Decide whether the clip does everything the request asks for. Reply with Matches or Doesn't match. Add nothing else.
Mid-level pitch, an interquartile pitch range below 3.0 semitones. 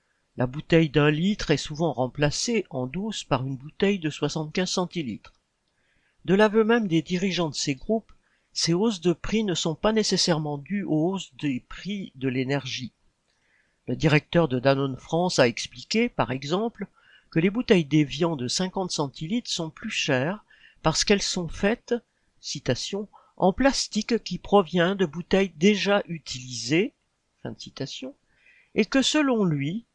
Doesn't match